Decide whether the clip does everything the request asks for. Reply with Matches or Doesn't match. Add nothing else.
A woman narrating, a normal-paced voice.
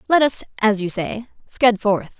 Matches